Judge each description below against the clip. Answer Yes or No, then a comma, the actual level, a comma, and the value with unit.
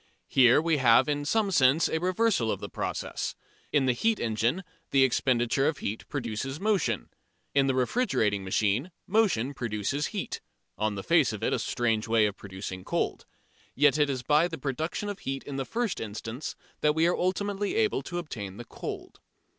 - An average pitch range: No, wide, 7.3 semitones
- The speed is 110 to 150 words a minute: No, average, 185 wpm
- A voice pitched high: No, low, 135 Hz